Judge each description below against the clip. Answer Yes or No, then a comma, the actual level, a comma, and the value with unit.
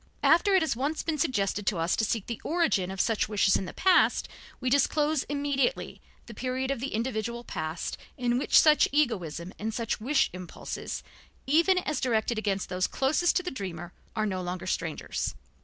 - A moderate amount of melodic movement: No, wide, 7.1 semitones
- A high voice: Yes, high, 235 Hz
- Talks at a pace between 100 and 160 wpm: No, average, 185 wpm